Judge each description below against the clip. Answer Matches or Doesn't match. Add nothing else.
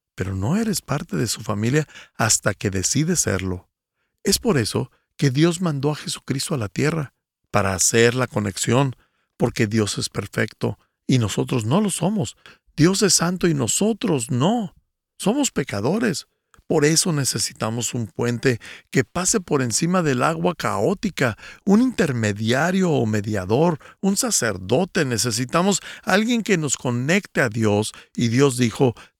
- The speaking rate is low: Doesn't match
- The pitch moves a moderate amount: Doesn't match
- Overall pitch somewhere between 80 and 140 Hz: Matches